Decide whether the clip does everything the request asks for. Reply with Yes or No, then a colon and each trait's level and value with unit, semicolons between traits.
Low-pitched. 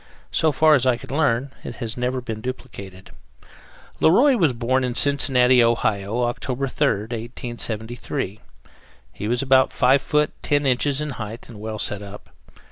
Yes: low, 125 Hz